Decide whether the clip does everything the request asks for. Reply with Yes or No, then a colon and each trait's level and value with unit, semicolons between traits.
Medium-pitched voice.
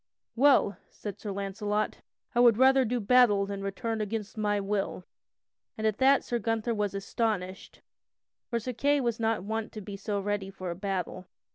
No: high, 210 Hz